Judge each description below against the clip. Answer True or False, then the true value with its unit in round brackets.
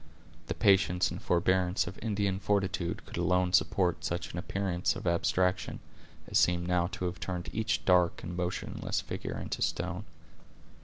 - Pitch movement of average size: False (1.4 semitones)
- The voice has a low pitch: True (90 Hz)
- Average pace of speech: True (155 wpm)